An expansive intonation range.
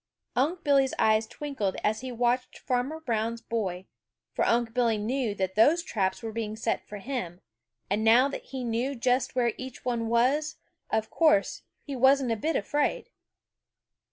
No: average, 3.4 semitones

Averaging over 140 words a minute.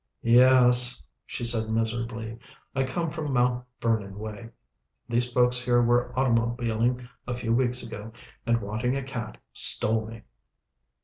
No: slow, 135 wpm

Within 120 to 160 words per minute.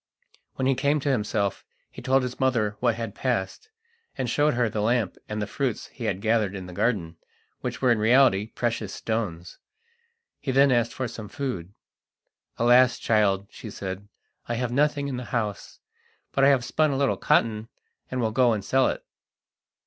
No: average, 185 wpm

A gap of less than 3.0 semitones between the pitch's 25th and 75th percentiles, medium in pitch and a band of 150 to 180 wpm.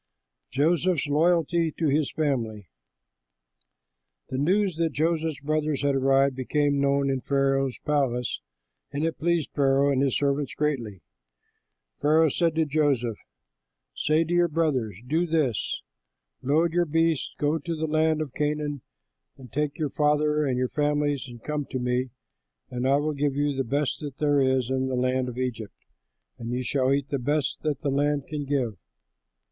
Yes: narrow, 2.6 semitones; medium, 145 Hz; average, 165 wpm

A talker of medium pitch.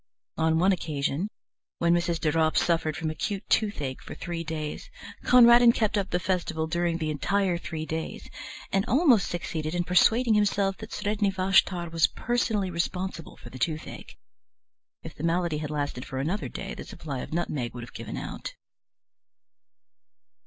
Yes: medium, 170 Hz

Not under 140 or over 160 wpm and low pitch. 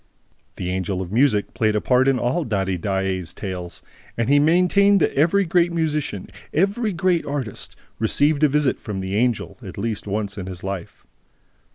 No: average, 175 wpm; low, 115 Hz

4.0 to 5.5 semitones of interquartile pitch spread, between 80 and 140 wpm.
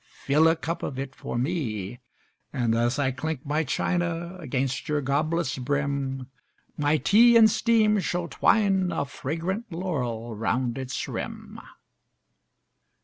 Yes: average, 5.0 semitones; slow, 135 wpm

